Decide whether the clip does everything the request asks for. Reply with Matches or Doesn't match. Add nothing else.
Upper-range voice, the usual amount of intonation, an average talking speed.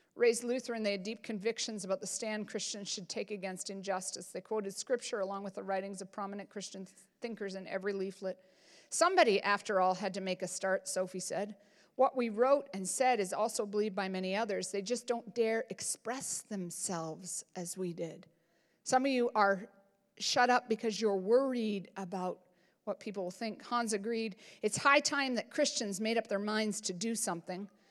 Matches